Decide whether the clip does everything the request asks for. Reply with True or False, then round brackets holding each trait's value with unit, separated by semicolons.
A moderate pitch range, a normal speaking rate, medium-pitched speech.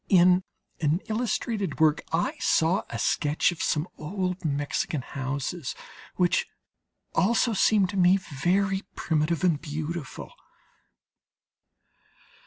False (3.9 semitones; 105 wpm; 175 Hz)